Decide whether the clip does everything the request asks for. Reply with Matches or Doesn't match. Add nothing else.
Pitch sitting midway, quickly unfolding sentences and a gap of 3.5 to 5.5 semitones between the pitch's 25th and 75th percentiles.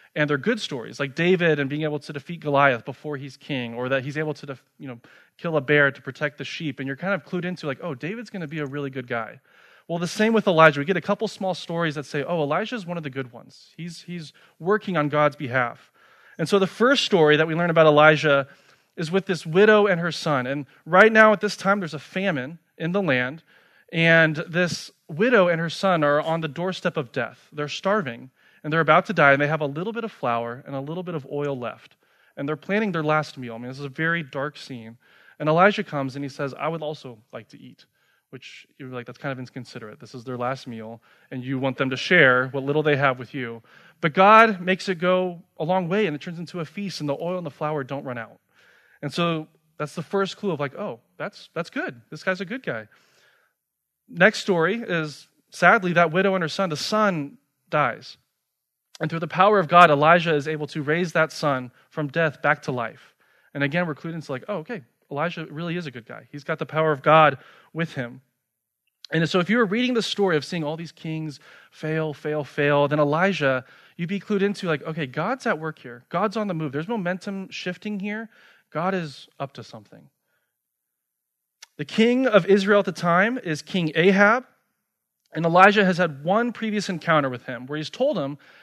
Matches